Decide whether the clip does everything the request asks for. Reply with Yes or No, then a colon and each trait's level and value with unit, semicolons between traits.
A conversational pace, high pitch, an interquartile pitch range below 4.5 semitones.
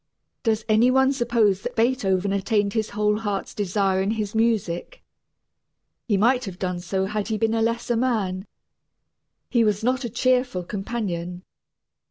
Yes: average, 155 wpm; high, 215 Hz; average, 3.3 semitones